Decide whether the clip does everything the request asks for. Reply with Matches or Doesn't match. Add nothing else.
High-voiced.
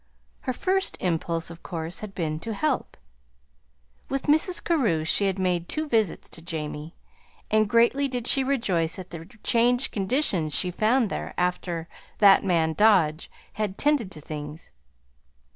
Matches